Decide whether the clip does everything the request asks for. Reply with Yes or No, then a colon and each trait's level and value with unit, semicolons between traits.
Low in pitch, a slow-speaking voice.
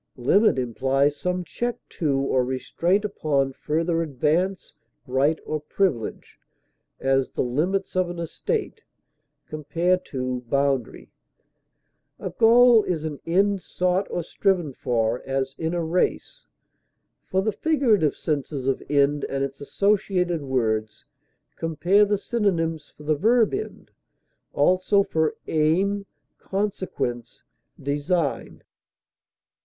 No: medium, 160 Hz; slow, 115 wpm